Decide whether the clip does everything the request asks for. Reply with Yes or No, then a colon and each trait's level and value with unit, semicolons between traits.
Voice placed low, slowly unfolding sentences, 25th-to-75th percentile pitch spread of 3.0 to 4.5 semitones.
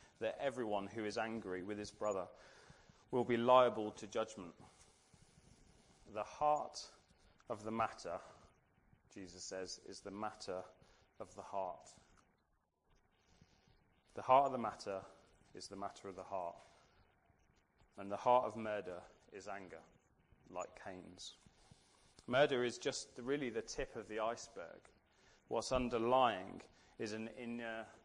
Yes: low, 105 Hz; slow, 130 wpm; average, 3.9 semitones